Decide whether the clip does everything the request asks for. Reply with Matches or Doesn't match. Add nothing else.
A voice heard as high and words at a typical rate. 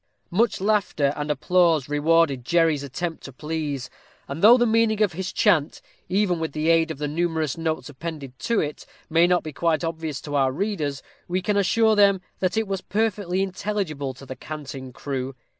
Doesn't match